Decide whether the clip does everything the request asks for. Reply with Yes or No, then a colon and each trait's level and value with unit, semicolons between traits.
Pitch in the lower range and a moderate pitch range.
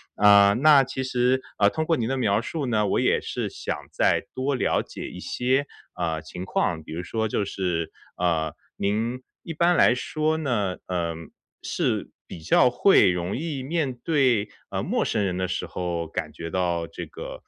No: low, 110 Hz; wide, 6.7 semitones